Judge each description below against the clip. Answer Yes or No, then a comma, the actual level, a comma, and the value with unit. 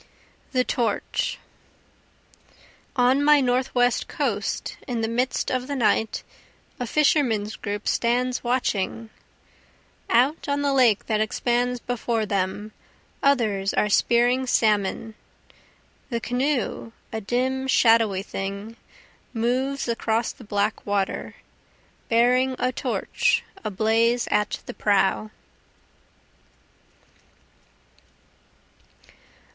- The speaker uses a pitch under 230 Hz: No, high, 235 Hz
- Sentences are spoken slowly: Yes, slow, 95 wpm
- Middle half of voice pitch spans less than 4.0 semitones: Yes, average, 3.0 semitones